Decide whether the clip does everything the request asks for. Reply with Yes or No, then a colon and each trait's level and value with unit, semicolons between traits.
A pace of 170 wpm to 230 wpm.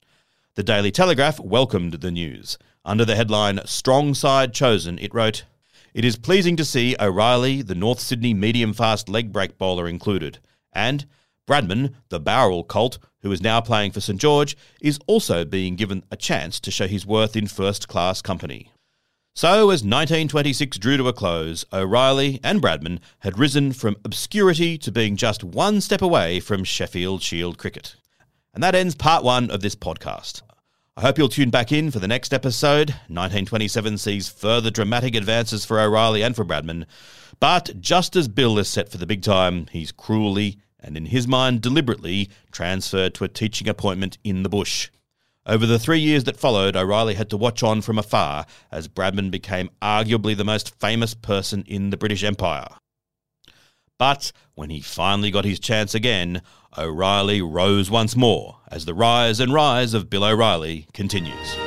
Yes: average, 175 wpm